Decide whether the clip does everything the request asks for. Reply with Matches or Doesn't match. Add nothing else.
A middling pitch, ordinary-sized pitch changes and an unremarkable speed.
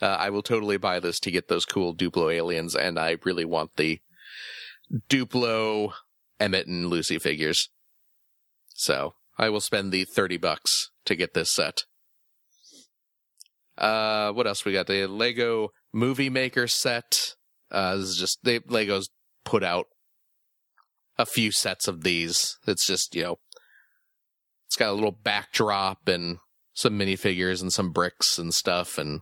Doesn't match